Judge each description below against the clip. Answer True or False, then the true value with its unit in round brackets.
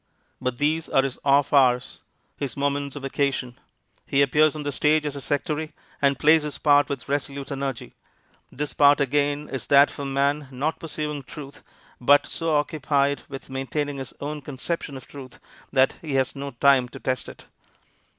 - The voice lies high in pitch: False (140 Hz)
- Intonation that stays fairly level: True (1.5 semitones)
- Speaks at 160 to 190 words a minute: True (180 wpm)